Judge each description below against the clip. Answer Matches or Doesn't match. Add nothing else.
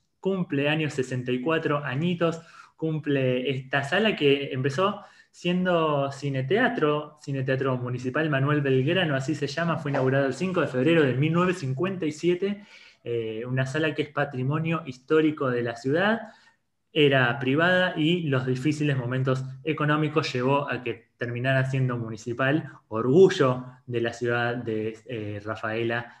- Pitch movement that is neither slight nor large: Matches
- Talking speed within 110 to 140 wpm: Matches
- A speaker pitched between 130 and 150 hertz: Matches